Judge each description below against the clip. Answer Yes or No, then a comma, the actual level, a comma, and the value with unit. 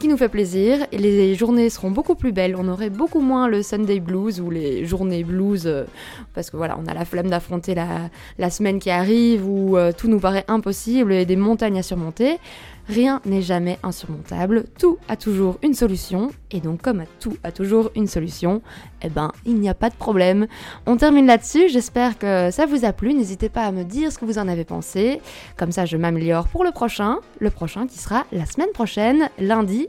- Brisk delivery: Yes, fast, 215 wpm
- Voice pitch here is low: No, high, 205 Hz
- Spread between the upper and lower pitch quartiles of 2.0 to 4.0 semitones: No, average, 4.5 semitones